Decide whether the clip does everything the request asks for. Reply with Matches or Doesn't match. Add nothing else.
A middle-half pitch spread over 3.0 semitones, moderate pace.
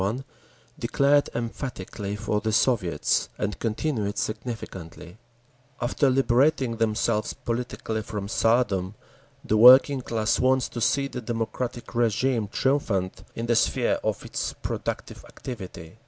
Doesn't match